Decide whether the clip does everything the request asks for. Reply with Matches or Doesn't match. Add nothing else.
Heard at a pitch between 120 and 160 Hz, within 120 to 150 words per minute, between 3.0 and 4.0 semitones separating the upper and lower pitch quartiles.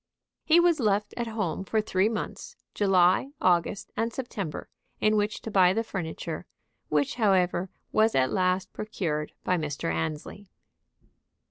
Doesn't match